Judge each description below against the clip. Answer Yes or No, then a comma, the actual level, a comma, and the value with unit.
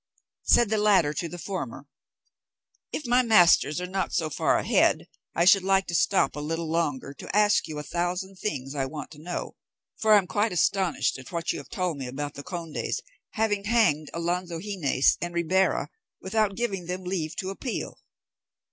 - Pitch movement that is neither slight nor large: Yes, average, 4.1 semitones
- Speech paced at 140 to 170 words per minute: No, average, 185 wpm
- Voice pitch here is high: No, medium, 180 Hz